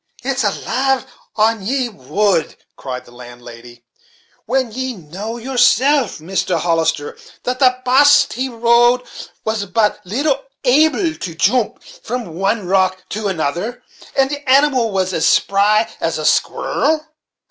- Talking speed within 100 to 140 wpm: Yes, slow, 135 wpm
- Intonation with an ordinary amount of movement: No, wide, 5.8 semitones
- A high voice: Yes, high, 225 Hz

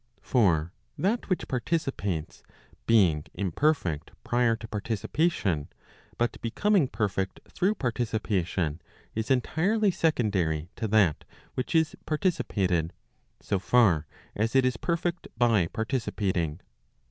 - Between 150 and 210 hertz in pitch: No, low, 110 Hz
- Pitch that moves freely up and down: Yes, wide, 7.5 semitones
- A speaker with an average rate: No, slow, 105 wpm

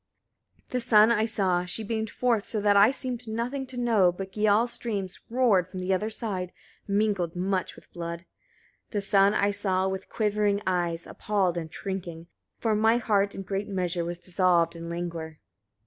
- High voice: Yes, high, 200 Hz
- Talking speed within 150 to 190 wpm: Yes, average, 180 wpm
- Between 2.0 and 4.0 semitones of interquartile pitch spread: Yes, average, 3.3 semitones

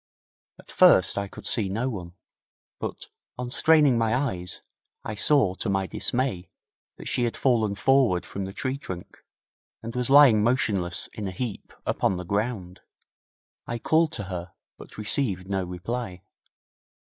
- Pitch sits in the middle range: No, low, 105 Hz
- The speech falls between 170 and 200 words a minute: No, average, 155 wpm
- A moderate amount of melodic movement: Yes, average, 5.0 semitones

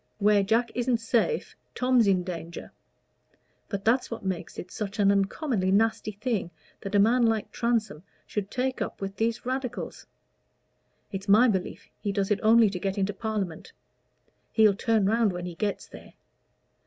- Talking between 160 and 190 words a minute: Yes, average, 165 wpm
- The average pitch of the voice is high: Yes, high, 210 Hz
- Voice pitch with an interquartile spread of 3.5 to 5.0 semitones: No, average, 2.9 semitones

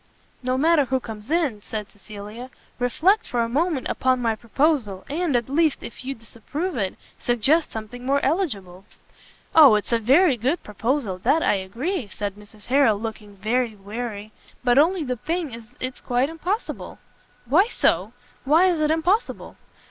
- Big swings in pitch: Yes, wide, 6.2 semitones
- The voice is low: No, very high, 250 Hz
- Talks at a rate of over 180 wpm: No, average, 165 wpm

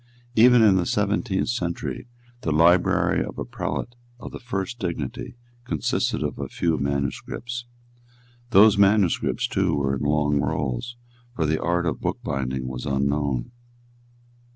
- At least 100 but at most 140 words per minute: Yes, slow, 135 wpm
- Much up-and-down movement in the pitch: Yes, wide, 6.6 semitones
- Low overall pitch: Yes, very low, 85 Hz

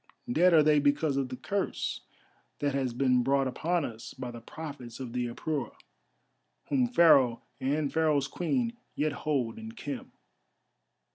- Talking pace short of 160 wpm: Yes, average, 150 wpm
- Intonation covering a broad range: No, average, 4.1 semitones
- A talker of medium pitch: Yes, medium, 145 Hz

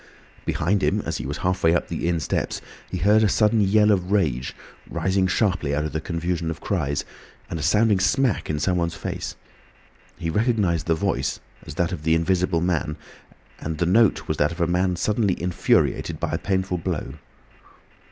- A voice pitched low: Yes, very low, 90 Hz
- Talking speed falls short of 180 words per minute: No, average, 185 wpm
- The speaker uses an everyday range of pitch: Yes, average, 3.2 semitones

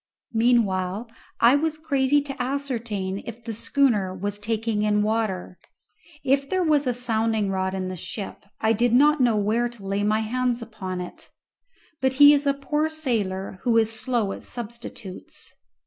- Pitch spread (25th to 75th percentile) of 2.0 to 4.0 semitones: No, average, 4.4 semitones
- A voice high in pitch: Yes, high, 230 Hz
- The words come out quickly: No, average, 165 wpm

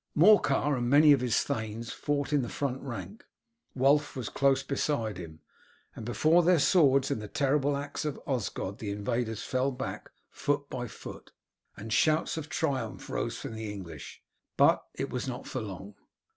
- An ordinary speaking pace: Yes, average, 170 wpm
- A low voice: Yes, low, 130 Hz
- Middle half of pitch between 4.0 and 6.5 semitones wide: Yes, average, 4.4 semitones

